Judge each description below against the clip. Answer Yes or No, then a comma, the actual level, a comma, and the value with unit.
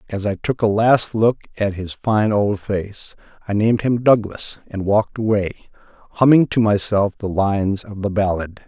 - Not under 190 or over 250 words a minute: No, average, 180 wpm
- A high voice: No, low, 105 Hz